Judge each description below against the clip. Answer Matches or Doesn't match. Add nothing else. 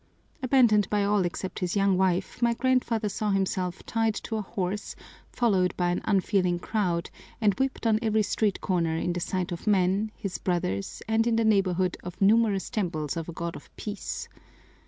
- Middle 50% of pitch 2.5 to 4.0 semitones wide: Matches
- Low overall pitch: Doesn't match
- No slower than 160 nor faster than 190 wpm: Matches